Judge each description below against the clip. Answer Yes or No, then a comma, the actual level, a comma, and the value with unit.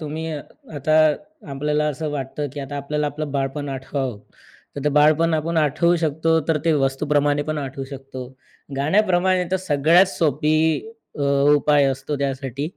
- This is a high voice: No, medium, 150 Hz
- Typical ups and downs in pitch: No, narrow, 2.3 semitones